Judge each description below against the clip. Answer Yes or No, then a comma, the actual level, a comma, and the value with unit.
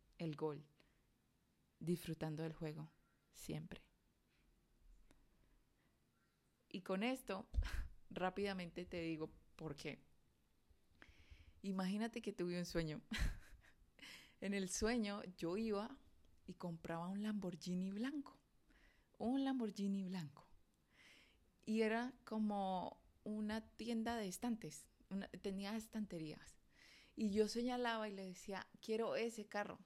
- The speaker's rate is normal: No, slow, 100 wpm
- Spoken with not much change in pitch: No, average, 4.1 semitones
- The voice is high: Yes, high, 195 Hz